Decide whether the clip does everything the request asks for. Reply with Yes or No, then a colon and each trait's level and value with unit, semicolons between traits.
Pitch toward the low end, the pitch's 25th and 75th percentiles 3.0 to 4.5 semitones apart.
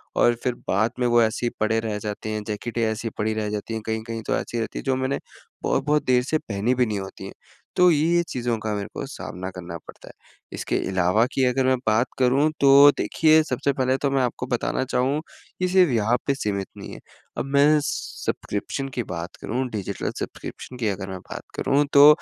Yes: low, 120 Hz; average, 4.1 semitones